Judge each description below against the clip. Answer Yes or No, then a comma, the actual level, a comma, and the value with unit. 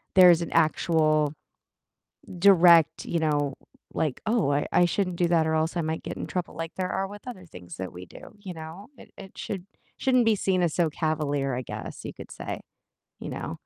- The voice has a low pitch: No, medium, 165 Hz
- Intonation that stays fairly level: No, average, 3.2 semitones